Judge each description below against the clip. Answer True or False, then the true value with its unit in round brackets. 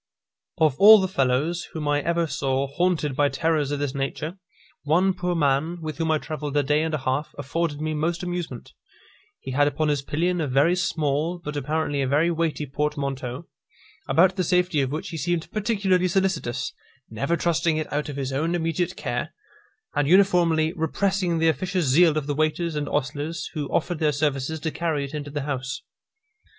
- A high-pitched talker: False (155 Hz)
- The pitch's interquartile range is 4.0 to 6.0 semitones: False (3.1 semitones)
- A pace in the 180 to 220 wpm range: True (185 wpm)